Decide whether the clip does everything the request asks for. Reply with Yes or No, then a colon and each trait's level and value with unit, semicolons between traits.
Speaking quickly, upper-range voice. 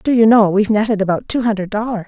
Yes: fast, 260 wpm; high, 210 Hz